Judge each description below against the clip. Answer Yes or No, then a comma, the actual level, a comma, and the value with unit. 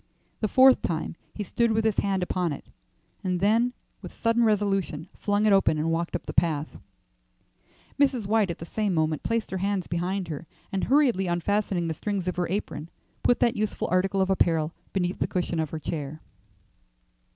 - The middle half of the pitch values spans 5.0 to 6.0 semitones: No, average, 4.0 semitones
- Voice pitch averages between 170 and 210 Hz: Yes, high, 190 Hz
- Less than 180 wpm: No, average, 185 wpm